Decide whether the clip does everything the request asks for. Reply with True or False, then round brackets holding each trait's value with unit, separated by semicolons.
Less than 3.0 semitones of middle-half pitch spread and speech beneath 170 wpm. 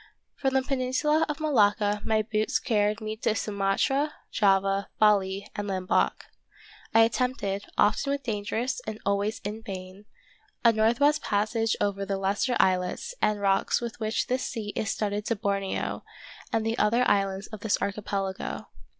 True (2.6 semitones; 155 wpm)